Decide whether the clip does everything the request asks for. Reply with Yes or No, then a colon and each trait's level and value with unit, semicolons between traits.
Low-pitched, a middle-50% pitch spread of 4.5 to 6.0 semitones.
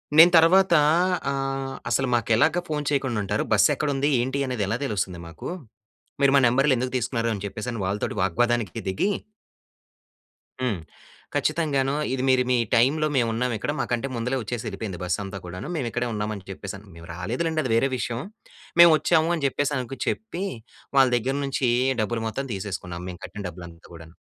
Yes: low, 120 Hz; average, 5.1 semitones